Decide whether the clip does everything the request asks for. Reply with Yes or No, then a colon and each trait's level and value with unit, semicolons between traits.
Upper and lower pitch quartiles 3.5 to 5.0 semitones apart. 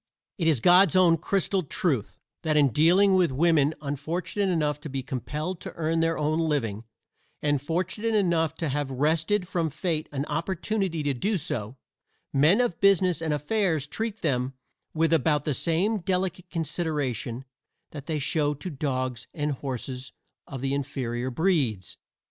Yes: average, 4.1 semitones